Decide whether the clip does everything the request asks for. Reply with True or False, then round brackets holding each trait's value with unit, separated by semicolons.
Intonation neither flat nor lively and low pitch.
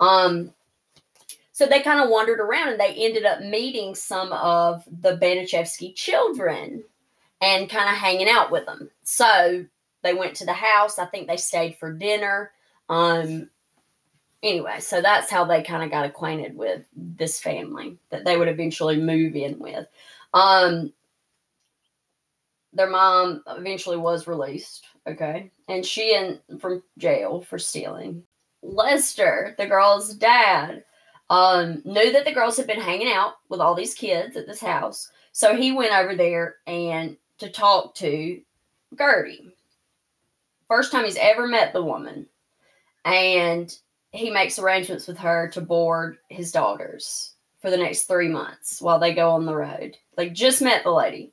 False (3.6 semitones; 180 Hz)